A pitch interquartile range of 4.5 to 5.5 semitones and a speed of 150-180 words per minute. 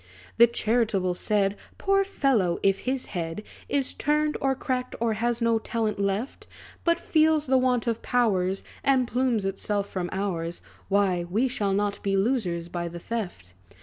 Yes: average, 4.8 semitones; average, 160 wpm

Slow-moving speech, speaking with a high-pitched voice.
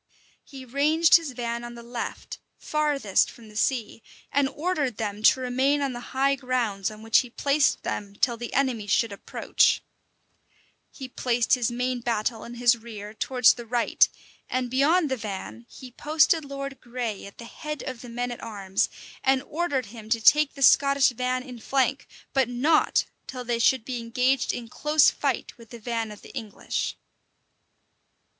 No: average, 175 wpm; high, 245 Hz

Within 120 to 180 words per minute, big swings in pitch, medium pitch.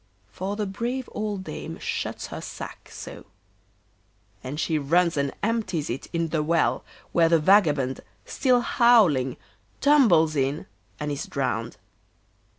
Yes: slow, 135 wpm; wide, 6.0 semitones; medium, 165 Hz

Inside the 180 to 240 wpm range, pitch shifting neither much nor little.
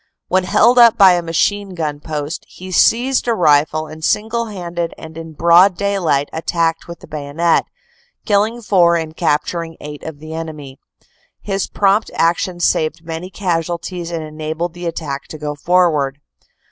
No: average, 160 wpm; average, 3.0 semitones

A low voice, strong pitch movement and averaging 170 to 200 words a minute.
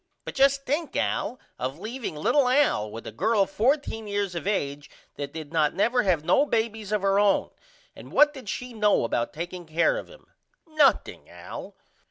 No: high, 205 Hz; wide, 8.1 semitones; average, 185 wpm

